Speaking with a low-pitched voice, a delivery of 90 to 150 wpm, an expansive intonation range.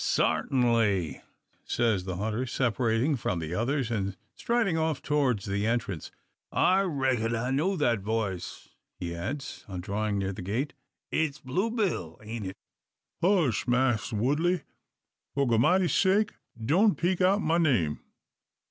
Yes: low, 120 Hz; average, 140 wpm; wide, 7.4 semitones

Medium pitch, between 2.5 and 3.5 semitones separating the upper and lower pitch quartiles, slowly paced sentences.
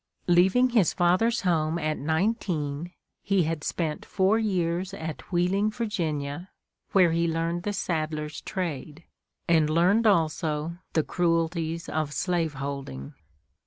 Yes: medium, 170 Hz; average, 3.2 semitones; slow, 125 wpm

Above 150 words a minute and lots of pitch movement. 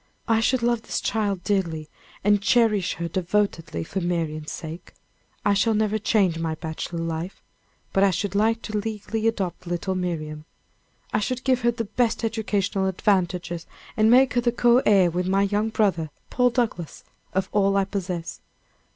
No: average, 170 wpm; average, 4.2 semitones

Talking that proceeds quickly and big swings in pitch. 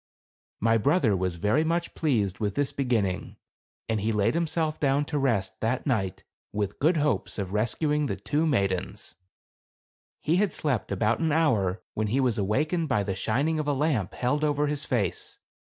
No: average, 175 wpm; wide, 6.5 semitones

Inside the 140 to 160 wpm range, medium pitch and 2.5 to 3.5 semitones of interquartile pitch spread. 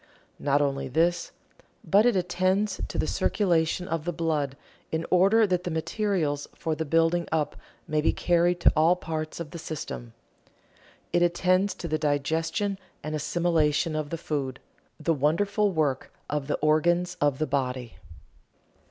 Yes: average, 155 wpm; medium, 160 Hz; average, 2.9 semitones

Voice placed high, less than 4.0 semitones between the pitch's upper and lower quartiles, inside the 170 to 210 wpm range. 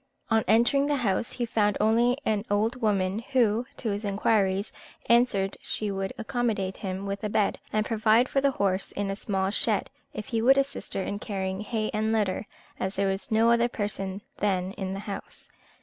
Yes: high, 210 Hz; average, 2.8 semitones; average, 195 wpm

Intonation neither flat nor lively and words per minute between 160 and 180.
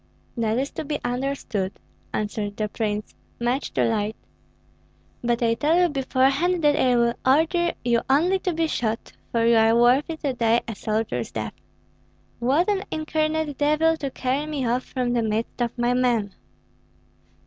Yes: average, 4.6 semitones; average, 165 wpm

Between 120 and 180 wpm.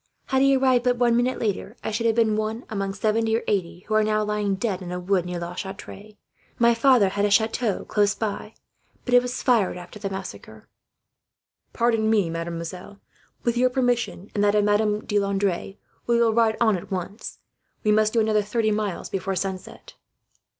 No: average, 190 wpm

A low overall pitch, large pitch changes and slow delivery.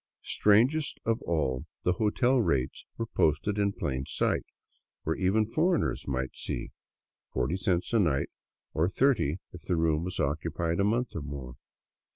No: very low, 90 Hz; wide, 7.0 semitones; average, 155 wpm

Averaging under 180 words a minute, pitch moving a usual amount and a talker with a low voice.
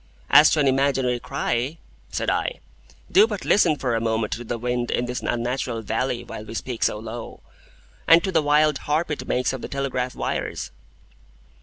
No: average, 185 wpm; average, 3.7 semitones; low, 125 Hz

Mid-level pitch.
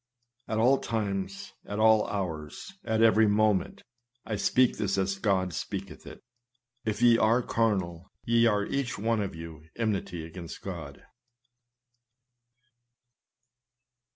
No: low, 105 Hz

